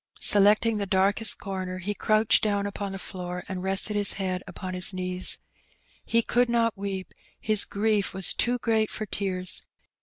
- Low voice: No, high, 200 Hz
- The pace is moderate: Yes, average, 175 wpm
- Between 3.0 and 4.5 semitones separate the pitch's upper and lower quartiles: No, narrow, 2.5 semitones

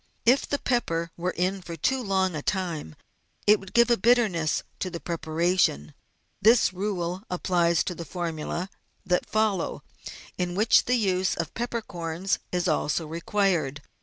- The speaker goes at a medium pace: Yes, average, 155 wpm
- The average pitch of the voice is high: No, medium, 180 Hz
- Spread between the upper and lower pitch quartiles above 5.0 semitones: No, average, 3.5 semitones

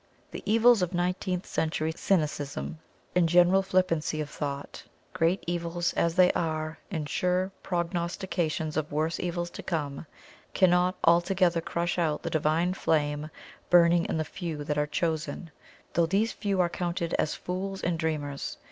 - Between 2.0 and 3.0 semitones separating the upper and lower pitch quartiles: Yes, narrow, 2.5 semitones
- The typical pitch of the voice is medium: Yes, medium, 170 Hz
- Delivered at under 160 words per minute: Yes, average, 150 wpm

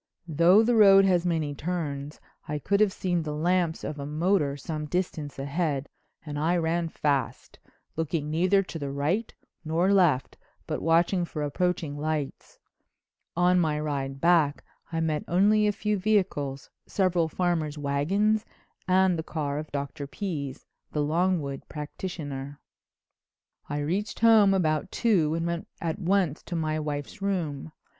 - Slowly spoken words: No, average, 150 wpm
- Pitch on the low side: No, medium, 165 Hz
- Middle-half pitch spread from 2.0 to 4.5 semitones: Yes, average, 3.9 semitones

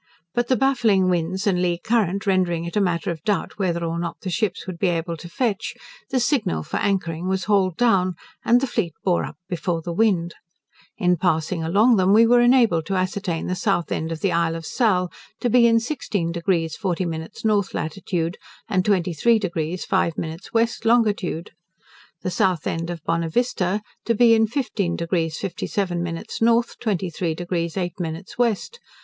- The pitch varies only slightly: No, average, 4.2 semitones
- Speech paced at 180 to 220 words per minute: Yes, average, 185 wpm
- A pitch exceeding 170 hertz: Yes, medium, 185 Hz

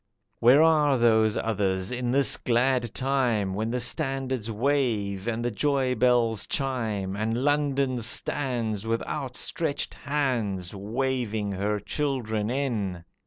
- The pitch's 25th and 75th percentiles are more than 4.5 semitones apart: No, average, 4.0 semitones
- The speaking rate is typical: No, slow, 120 wpm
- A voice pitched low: Yes, low, 120 Hz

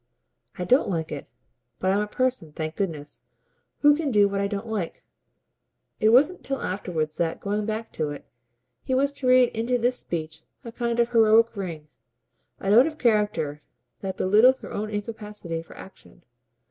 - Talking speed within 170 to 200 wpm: Yes, average, 175 wpm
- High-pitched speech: Yes, high, 210 Hz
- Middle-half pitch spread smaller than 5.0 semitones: No, wide, 5.5 semitones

